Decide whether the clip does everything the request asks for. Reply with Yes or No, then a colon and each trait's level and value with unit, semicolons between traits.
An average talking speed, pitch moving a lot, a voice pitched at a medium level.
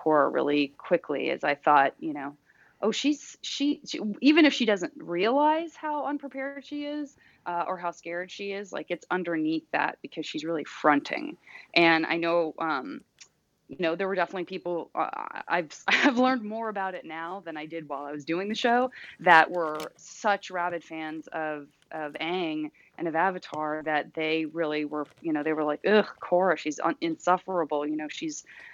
Yes: average, 185 wpm; wide, 8.4 semitones; medium, 175 Hz